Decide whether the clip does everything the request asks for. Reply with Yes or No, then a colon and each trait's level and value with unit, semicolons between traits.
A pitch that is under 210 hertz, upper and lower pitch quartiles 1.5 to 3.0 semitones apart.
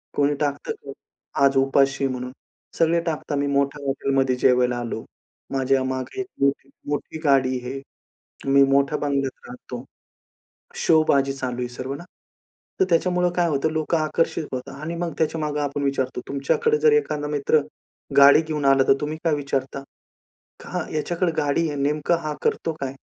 Yes: medium, 140 Hz; narrow, 2.5 semitones